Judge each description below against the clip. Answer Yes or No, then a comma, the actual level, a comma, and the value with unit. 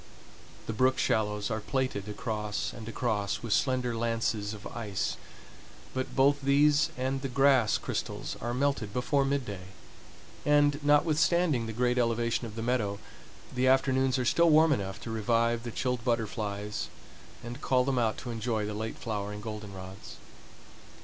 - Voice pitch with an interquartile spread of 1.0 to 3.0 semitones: No, average, 3.7 semitones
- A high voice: No, low, 120 Hz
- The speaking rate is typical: Yes, average, 150 wpm